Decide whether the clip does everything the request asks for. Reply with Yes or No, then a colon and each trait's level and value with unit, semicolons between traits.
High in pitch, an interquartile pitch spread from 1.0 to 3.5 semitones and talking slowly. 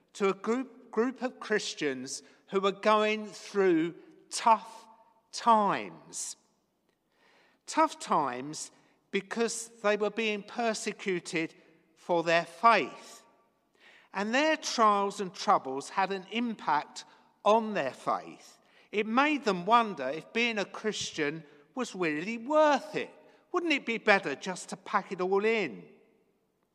Yes: high, 215 Hz; average, 3.1 semitones; slow, 125 wpm